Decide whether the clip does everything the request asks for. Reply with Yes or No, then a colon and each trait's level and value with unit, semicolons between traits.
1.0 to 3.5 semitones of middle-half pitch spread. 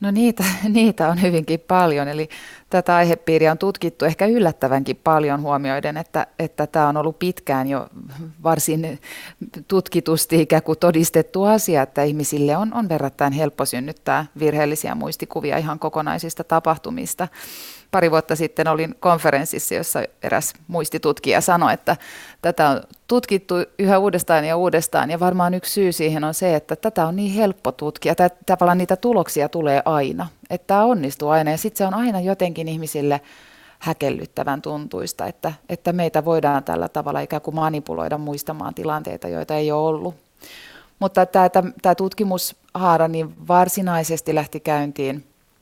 Yes: average, 3.2 semitones